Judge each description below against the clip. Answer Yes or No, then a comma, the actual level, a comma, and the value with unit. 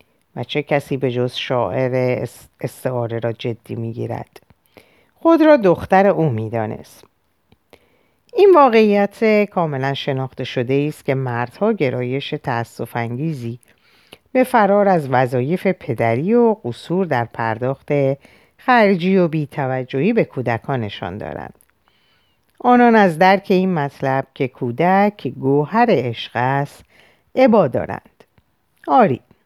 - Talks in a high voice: No, medium, 140 Hz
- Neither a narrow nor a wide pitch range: No, wide, 7.6 semitones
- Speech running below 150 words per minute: Yes, average, 115 wpm